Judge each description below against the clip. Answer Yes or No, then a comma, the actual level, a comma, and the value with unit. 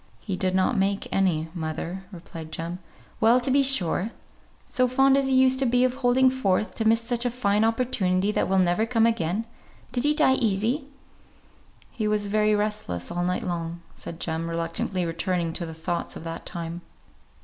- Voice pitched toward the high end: Yes, high, 200 Hz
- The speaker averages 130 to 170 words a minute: No, average, 185 wpm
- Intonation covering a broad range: Yes, wide, 6.0 semitones